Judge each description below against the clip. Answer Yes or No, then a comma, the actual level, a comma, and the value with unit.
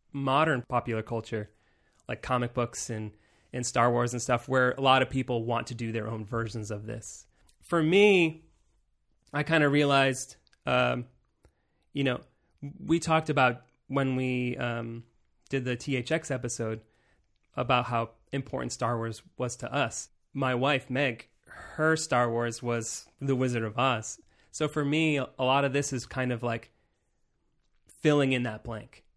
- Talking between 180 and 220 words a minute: No, average, 160 wpm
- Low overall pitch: Yes, low, 125 Hz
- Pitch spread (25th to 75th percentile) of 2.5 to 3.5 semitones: Yes, average, 3.2 semitones